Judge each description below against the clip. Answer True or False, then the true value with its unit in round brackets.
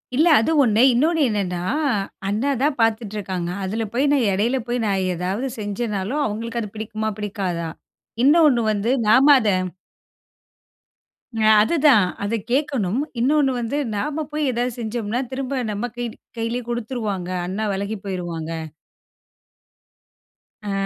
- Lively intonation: False (4.4 semitones)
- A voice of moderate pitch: False (225 Hz)